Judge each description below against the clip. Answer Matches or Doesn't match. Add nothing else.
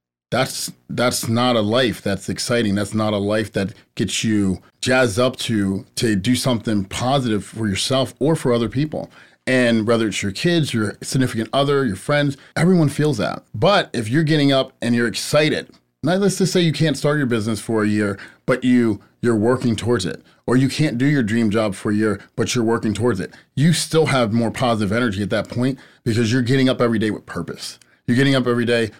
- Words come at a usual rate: Doesn't match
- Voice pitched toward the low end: Matches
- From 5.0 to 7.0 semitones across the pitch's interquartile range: Doesn't match